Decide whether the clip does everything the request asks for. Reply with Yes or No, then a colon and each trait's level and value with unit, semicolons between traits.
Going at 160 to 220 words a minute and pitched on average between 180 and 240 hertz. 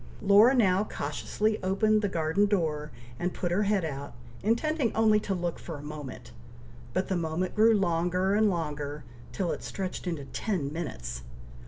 Yes: average, 165 wpm; medium, 185 Hz